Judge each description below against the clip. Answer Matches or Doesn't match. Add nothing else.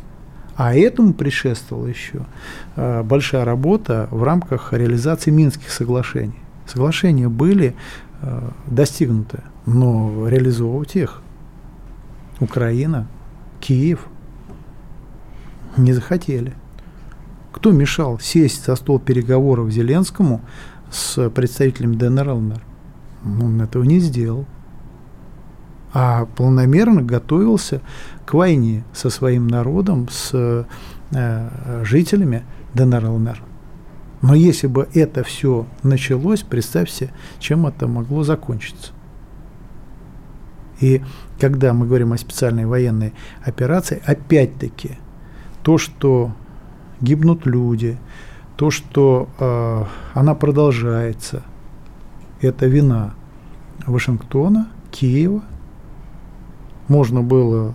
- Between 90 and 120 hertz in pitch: Doesn't match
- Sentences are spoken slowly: Matches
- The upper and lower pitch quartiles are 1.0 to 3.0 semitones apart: Doesn't match